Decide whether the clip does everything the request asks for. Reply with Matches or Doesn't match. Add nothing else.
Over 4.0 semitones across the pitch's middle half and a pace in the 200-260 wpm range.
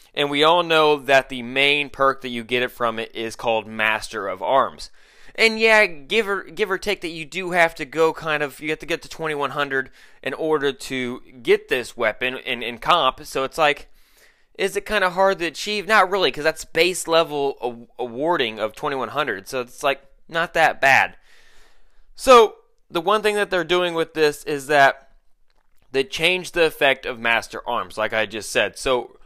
Matches